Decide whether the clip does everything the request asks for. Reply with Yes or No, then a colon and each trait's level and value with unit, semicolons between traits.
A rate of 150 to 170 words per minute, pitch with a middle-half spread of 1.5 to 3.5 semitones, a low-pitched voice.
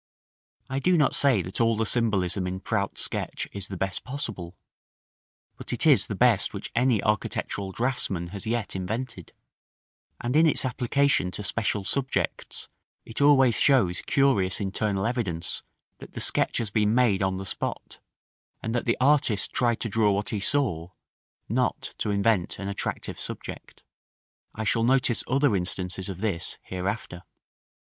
No: average, 155 wpm; average, 4.5 semitones; low, 110 Hz